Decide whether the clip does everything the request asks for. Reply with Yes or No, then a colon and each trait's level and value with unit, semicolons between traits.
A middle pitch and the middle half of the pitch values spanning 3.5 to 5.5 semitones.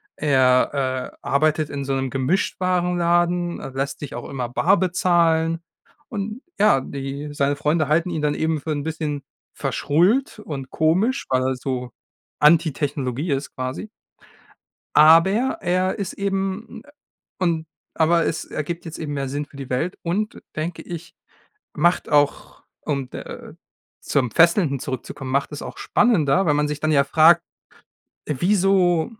Yes: medium, 155 Hz; average, 4.1 semitones